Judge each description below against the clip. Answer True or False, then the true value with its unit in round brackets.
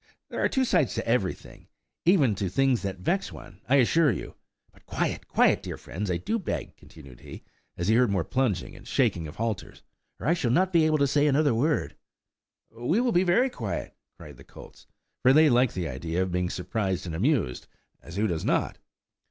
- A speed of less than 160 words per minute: False (200 wpm)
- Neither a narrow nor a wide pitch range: False (8.3 semitones)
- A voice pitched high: False (115 Hz)